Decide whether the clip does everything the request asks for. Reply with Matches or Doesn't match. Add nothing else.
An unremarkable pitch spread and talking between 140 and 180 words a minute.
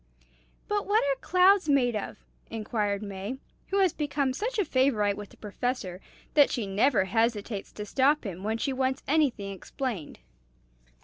Doesn't match